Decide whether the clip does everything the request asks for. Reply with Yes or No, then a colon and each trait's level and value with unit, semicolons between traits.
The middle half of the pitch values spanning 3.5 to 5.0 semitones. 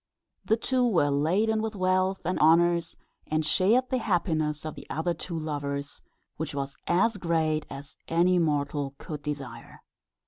Yes: average, 4.0 semitones